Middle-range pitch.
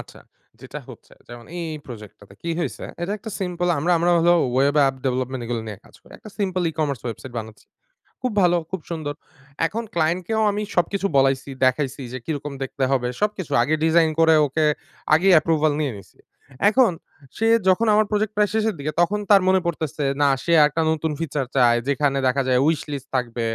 Yes: medium, 155 Hz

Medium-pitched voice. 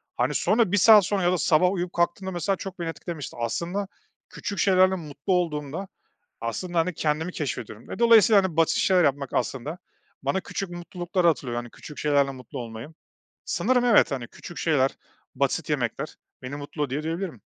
Yes: medium, 170 Hz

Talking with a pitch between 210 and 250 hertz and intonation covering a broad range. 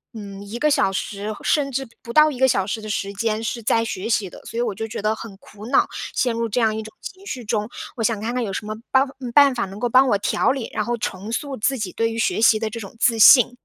No: high, 225 Hz; average, 2.7 semitones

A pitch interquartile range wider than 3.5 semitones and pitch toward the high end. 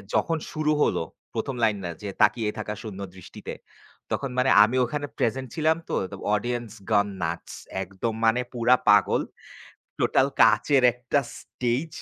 No: average, 4.0 semitones; low, 120 Hz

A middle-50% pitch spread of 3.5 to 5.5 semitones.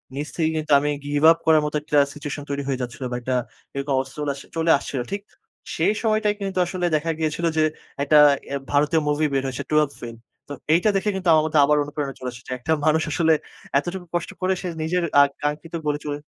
No: average, 2.8 semitones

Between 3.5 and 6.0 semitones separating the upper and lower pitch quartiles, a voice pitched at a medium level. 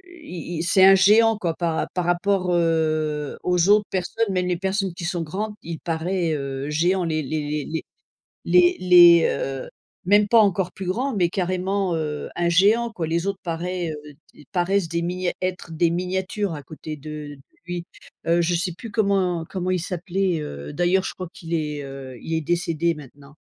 No: average, 2.9 semitones; medium, 175 Hz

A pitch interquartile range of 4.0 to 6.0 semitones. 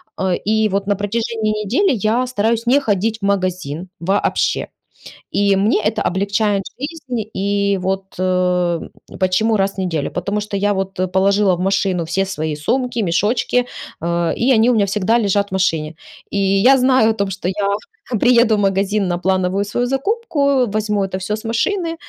No: average, 3.1 semitones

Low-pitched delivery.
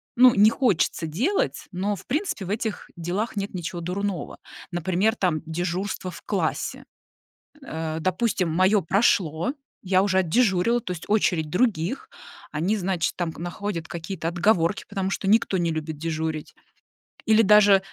No: medium, 185 Hz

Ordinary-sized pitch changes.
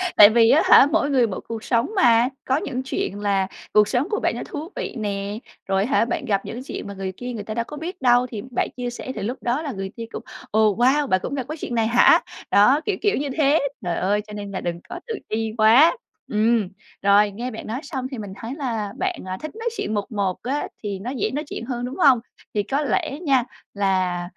Yes: average, 5.0 semitones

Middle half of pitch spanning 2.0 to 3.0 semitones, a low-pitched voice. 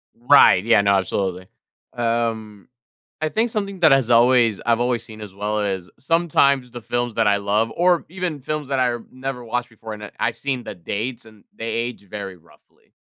No: average, 3.9 semitones; low, 115 Hz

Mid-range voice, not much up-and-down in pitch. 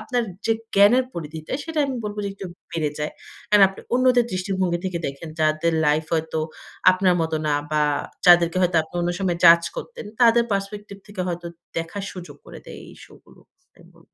No: medium, 180 Hz; average, 4.0 semitones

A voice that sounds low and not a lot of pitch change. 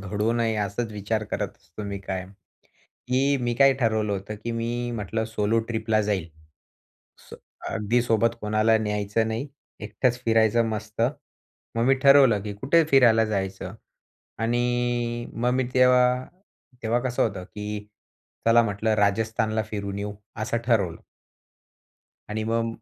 Yes: low, 110 Hz; narrow, 2.3 semitones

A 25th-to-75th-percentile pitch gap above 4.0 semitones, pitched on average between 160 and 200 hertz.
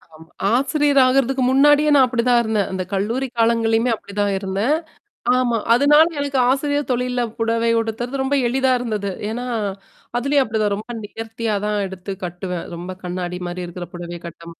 No: average, 5.0 semitones; high, 230 Hz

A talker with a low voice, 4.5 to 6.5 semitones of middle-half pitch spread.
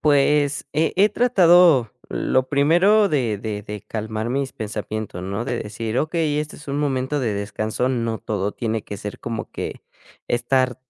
Yes: low, 125 Hz; average, 5.3 semitones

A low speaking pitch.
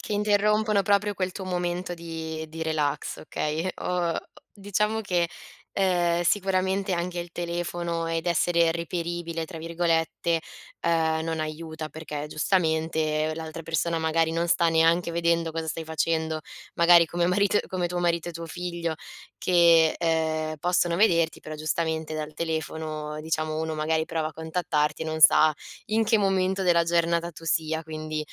No: medium, 165 Hz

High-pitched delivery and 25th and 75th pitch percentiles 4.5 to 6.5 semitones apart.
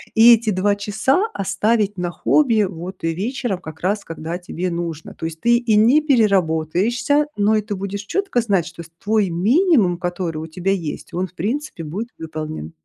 Yes: high, 195 Hz; average, 5.0 semitones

